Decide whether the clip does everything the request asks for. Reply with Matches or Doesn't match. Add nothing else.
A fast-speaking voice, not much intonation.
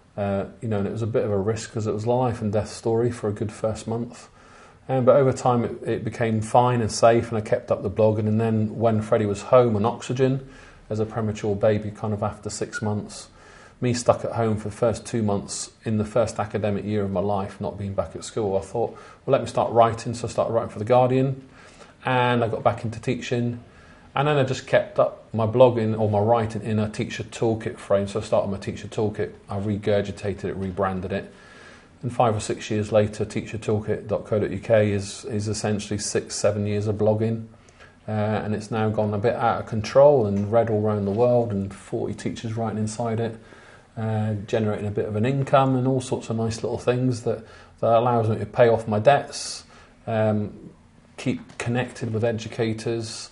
Matches